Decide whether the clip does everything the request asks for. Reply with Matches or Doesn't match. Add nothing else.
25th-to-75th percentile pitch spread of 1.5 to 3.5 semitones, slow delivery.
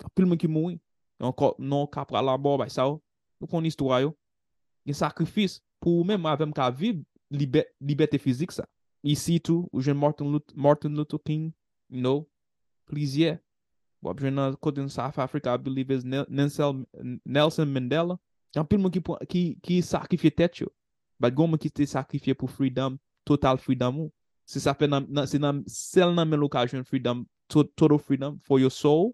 Matches